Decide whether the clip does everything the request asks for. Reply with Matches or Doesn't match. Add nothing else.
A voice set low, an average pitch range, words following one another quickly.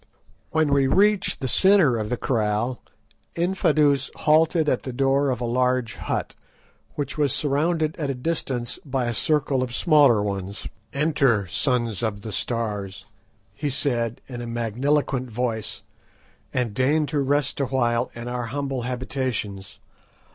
Doesn't match